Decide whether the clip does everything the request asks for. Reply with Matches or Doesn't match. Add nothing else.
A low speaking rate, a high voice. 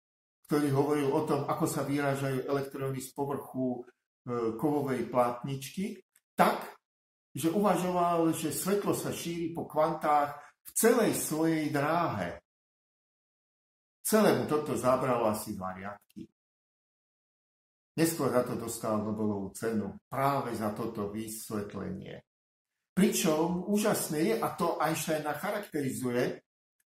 Doesn't match